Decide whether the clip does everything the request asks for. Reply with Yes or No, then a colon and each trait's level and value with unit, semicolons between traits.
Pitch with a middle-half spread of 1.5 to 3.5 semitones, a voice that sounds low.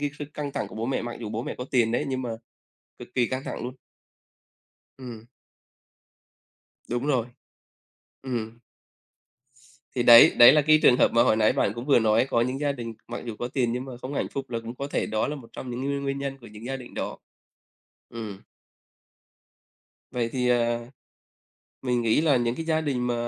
Yes: narrow, 2.4 semitones; low, 125 Hz